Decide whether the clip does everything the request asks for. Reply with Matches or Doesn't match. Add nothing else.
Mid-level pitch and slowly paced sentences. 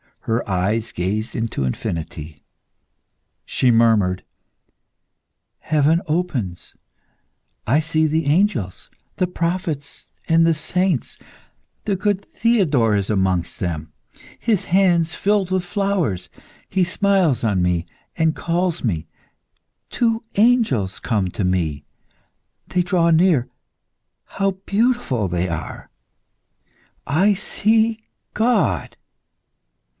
Matches